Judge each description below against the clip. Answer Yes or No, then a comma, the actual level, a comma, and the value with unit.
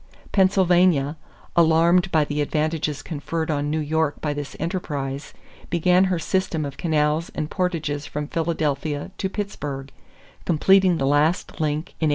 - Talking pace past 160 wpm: No, average, 145 wpm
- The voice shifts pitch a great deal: No, average, 3.2 semitones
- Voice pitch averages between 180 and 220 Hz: No, medium, 160 Hz